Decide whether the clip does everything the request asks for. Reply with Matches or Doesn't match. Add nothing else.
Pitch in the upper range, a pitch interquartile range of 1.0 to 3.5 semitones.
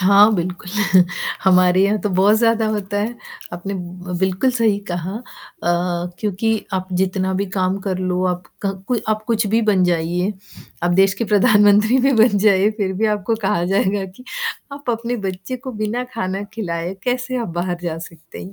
Matches